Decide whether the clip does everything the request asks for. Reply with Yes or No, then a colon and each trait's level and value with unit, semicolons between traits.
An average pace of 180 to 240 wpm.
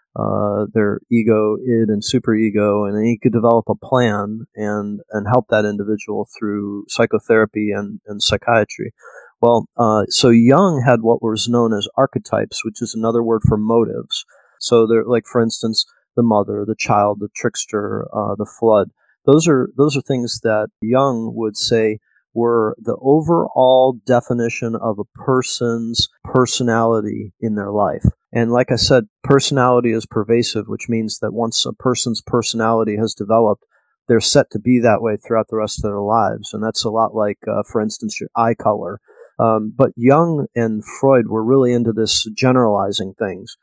No: average, 170 wpm